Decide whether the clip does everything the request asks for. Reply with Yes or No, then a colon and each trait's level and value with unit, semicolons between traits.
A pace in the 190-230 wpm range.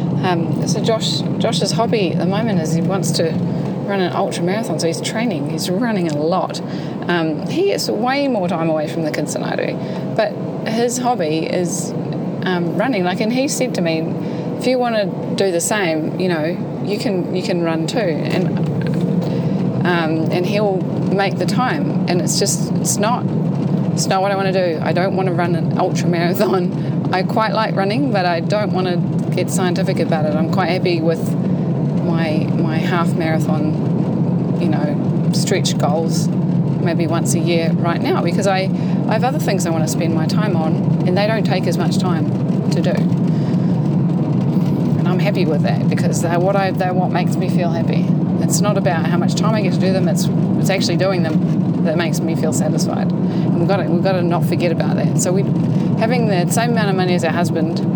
Yes: fast, 205 wpm